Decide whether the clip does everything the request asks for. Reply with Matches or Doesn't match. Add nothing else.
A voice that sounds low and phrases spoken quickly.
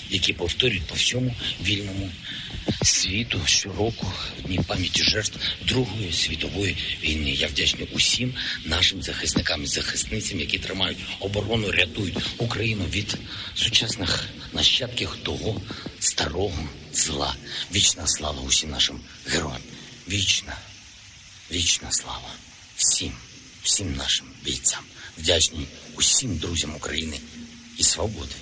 Doesn't match